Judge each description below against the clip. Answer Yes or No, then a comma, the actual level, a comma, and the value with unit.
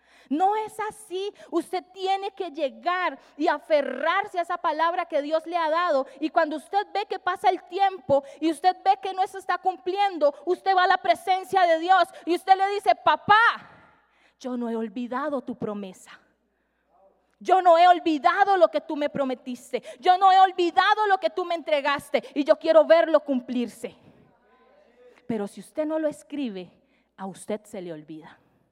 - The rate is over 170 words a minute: Yes, average, 180 wpm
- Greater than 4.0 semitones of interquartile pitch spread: Yes, average, 5.0 semitones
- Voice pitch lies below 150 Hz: No, very high, 330 Hz